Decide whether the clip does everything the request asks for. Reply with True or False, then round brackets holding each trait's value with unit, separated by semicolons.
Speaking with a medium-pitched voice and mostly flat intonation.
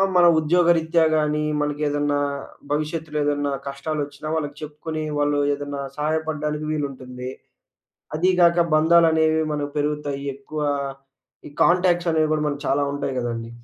True (150 Hz; 1.8 semitones)